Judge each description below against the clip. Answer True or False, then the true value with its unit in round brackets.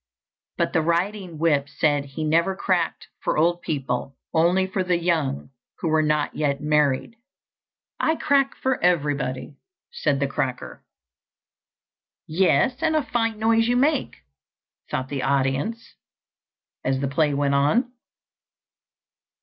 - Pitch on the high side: False (160 Hz)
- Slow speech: True (130 wpm)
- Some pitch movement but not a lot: False (5.8 semitones)